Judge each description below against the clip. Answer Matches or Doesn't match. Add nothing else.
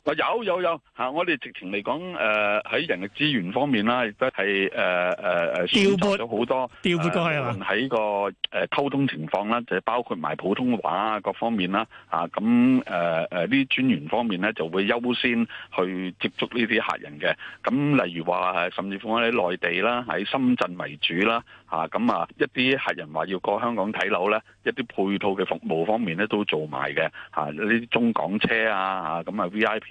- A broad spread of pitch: Matches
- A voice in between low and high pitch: Doesn't match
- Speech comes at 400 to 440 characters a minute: Doesn't match